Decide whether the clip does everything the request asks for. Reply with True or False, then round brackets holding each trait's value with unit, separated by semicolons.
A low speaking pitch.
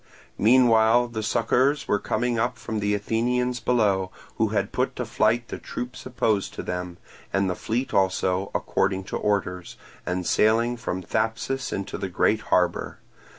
True (110 Hz)